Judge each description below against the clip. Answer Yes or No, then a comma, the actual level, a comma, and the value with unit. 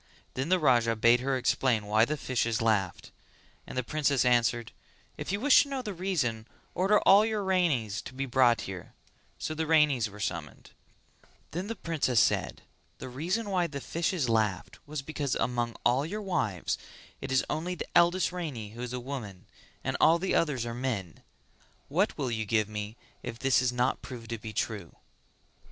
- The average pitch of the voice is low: Yes, low, 130 Hz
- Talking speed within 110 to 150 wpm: No, average, 185 wpm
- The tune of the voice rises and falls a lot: Yes, wide, 6.6 semitones